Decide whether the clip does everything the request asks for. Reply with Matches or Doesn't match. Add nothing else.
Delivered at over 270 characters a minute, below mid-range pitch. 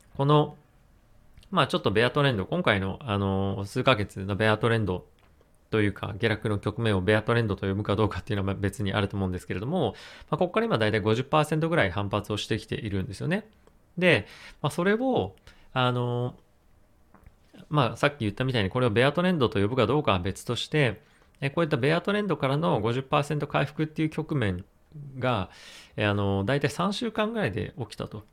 Matches